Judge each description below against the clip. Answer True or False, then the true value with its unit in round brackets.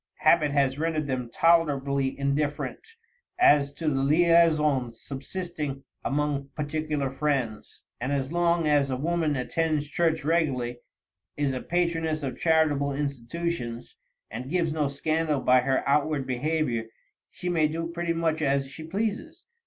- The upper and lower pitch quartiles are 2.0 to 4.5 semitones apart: True (3.2 semitones)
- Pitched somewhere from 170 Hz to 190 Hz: False (150 Hz)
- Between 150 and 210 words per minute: False (135 wpm)